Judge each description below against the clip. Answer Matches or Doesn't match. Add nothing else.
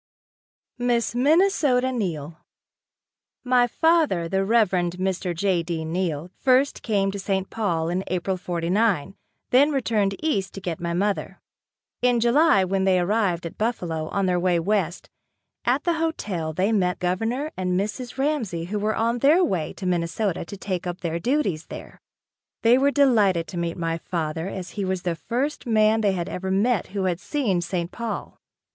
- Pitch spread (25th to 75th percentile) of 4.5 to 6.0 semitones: Matches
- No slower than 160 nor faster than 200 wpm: Matches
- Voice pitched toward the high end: Matches